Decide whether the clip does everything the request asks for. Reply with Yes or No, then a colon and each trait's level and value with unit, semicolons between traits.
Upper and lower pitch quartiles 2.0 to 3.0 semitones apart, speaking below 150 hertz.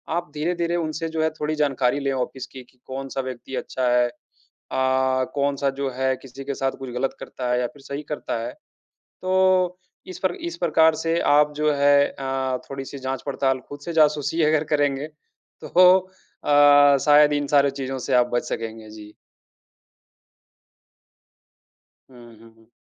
Yes: narrow, 2.5 semitones; medium, 140 Hz